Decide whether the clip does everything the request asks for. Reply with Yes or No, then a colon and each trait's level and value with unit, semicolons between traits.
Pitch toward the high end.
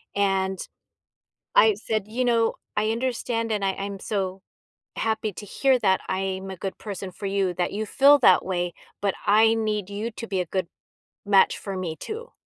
Yes: high, 200 Hz